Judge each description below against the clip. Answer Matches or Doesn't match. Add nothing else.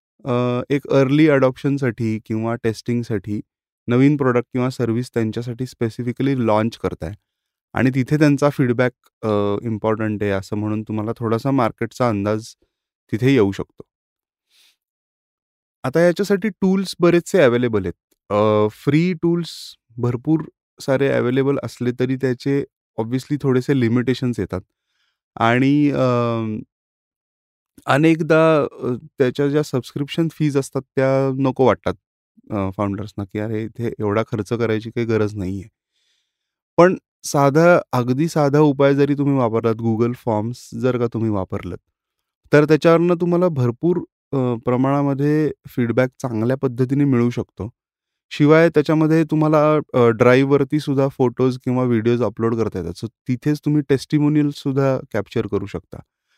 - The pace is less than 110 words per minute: Doesn't match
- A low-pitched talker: Matches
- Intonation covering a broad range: Doesn't match